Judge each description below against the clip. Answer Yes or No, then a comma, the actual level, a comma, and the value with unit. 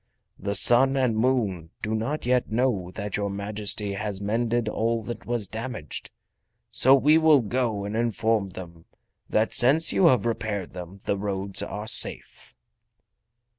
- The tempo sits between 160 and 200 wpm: No, average, 150 wpm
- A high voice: No, low, 110 Hz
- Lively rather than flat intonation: No, average, 3.3 semitones